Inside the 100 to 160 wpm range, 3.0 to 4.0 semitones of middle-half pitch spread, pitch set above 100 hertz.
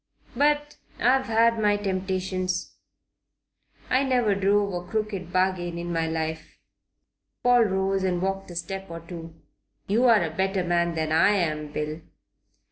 Yes: average, 140 wpm; average, 3.3 semitones; high, 190 Hz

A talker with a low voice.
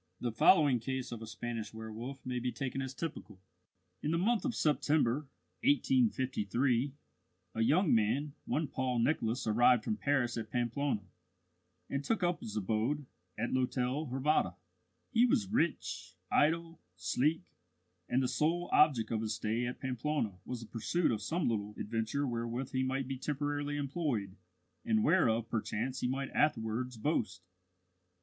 Yes: low, 130 Hz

